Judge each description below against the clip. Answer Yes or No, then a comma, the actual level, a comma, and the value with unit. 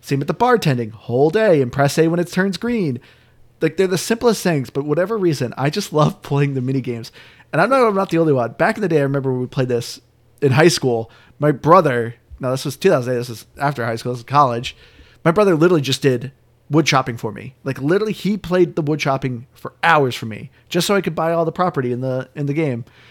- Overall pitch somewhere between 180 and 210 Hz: No, medium, 140 Hz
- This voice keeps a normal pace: No, fast, 250 wpm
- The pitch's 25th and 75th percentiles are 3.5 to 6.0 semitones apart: Yes, wide, 5.4 semitones